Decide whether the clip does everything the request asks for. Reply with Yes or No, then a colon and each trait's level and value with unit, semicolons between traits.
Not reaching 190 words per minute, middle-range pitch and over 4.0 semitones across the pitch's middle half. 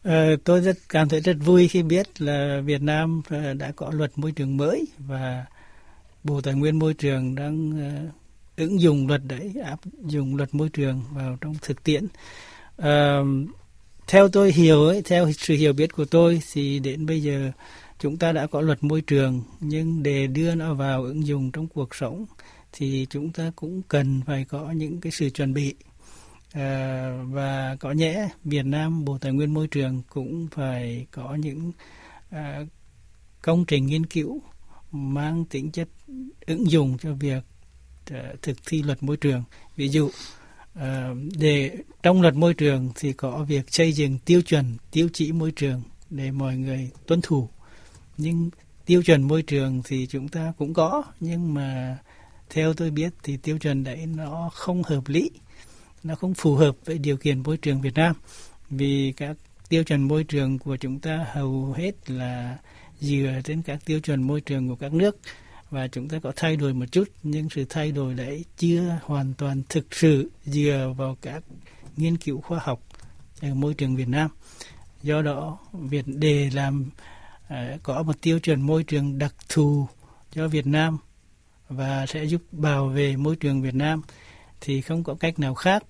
No: average, 175 wpm; medium, 145 Hz; average, 2.8 semitones